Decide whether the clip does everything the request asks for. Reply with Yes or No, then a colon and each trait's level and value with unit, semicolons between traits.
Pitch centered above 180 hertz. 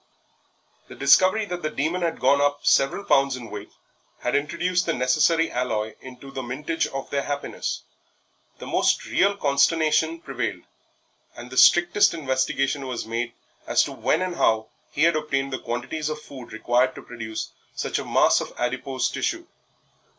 No: medium, 140 Hz